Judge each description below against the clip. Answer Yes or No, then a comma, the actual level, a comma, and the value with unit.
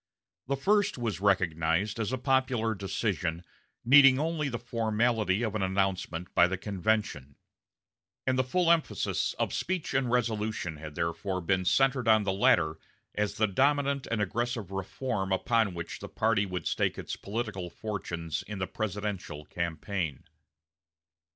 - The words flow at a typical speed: Yes, average, 145 wpm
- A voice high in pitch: No, low, 105 Hz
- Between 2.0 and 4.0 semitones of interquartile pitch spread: No, average, 4.8 semitones